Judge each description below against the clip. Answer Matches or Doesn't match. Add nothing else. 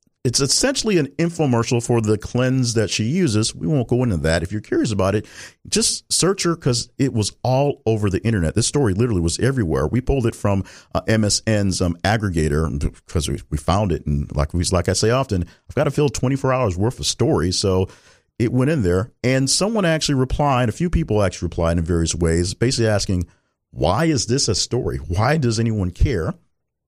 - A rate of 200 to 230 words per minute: Matches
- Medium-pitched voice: Doesn't match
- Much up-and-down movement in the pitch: Matches